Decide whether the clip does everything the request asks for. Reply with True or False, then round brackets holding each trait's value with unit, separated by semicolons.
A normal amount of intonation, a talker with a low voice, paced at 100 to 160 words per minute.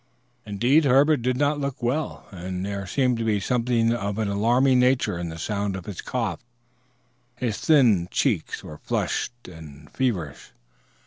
True (5.0 semitones; 115 Hz; 155 wpm)